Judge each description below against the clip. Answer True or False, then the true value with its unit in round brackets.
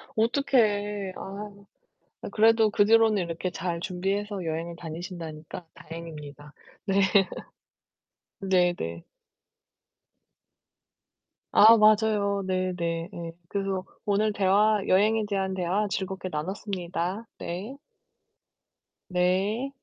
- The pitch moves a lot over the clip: False (3.2 semitones)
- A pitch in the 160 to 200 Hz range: True (190 Hz)